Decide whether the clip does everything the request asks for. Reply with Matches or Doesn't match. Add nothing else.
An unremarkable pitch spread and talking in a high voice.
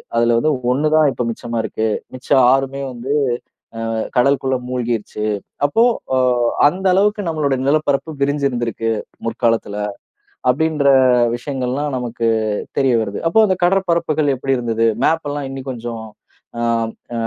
Doesn't match